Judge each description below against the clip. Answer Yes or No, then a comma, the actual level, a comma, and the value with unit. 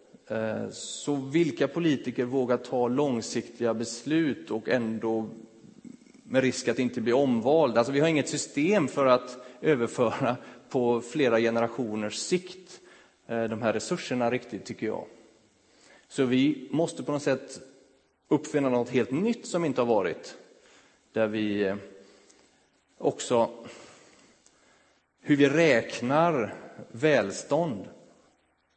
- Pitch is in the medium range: No, low, 125 Hz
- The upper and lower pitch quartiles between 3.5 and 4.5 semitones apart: Yes, average, 4.2 semitones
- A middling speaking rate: No, slow, 115 wpm